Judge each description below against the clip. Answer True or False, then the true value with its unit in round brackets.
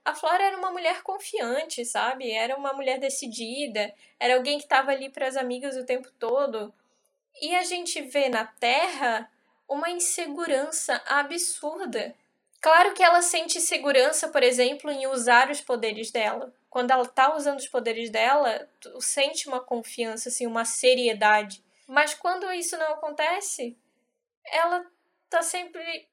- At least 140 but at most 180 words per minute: True (150 wpm)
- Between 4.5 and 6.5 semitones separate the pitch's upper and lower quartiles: True (5.1 semitones)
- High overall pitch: True (275 Hz)